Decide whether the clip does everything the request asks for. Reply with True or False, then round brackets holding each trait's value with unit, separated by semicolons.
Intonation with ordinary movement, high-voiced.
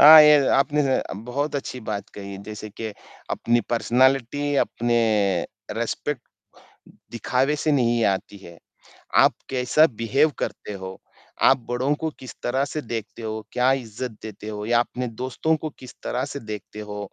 False (3.9 semitones; 120 Hz)